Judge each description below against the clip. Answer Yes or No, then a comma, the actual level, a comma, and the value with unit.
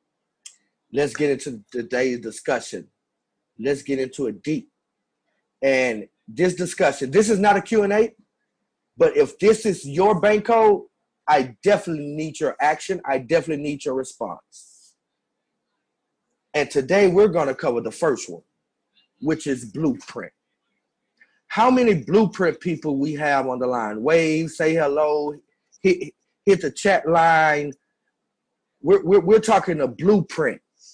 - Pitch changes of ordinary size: No, wide, 6.3 semitones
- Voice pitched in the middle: Yes, medium, 160 Hz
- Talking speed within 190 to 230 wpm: No, slow, 135 wpm